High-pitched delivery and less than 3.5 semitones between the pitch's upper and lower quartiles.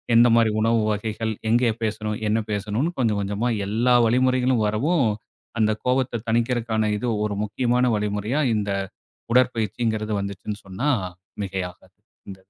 No: low, 110 Hz; average, 2.8 semitones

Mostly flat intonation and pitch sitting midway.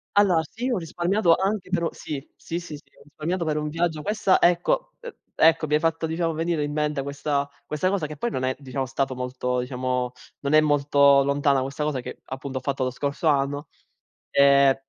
No: average, 3.3 semitones; medium, 150 Hz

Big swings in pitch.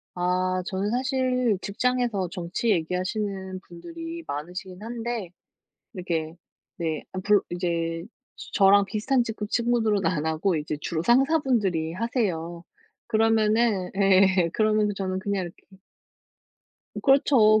No: average, 4.4 semitones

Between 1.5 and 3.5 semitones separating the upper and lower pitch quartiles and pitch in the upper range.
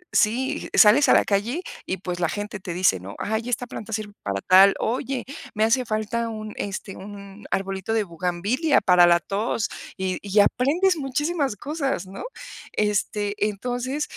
No: average, 4.4 semitones; high, 210 Hz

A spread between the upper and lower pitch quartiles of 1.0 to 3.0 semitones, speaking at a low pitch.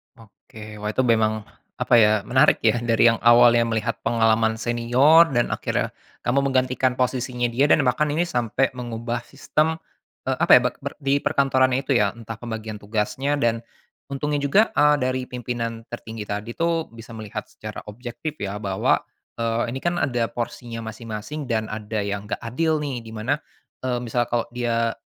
Yes: average, 2.7 semitones; low, 120 Hz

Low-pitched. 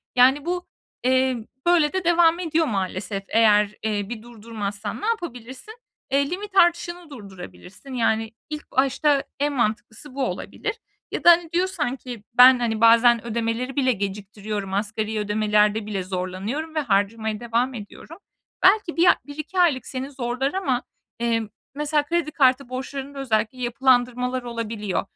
No: very high, 250 Hz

